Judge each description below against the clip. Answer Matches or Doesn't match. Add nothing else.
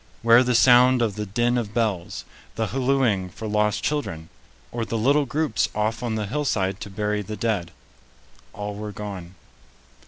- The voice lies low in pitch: Matches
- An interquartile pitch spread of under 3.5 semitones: Matches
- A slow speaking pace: Doesn't match